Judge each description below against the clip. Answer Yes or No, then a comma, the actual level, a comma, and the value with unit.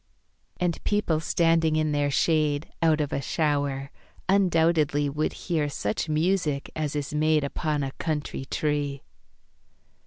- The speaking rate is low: Yes, slow, 130 wpm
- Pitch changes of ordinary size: No, narrow, 2.1 semitones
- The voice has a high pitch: No, medium, 150 Hz